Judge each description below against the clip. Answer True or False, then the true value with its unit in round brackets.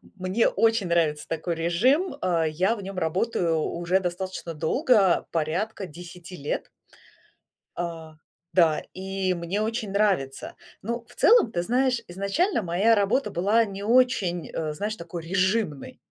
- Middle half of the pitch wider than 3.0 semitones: True (4.4 semitones)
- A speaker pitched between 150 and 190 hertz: True (185 Hz)